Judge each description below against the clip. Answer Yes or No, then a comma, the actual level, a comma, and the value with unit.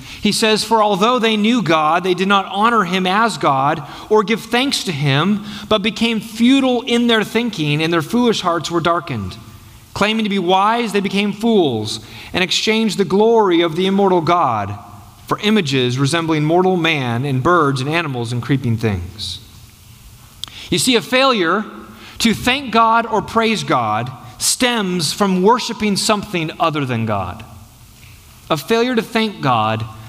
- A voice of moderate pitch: Yes, medium, 180 Hz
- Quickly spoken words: No, average, 160 wpm